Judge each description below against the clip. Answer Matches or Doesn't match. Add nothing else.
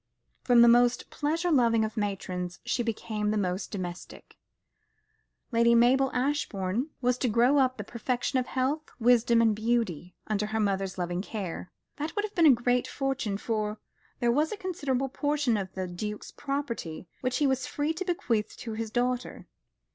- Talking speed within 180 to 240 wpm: Doesn't match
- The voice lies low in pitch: Doesn't match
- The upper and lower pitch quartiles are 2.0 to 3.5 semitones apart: Doesn't match